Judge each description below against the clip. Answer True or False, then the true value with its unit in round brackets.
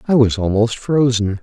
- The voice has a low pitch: True (115 Hz)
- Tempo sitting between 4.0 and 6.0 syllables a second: True (4.7 syllables/s)